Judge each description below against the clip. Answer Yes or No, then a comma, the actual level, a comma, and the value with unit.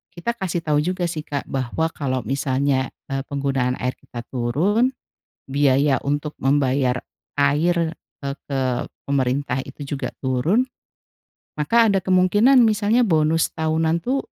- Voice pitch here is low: No, medium, 145 Hz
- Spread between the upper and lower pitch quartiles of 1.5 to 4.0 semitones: No, average, 4.6 semitones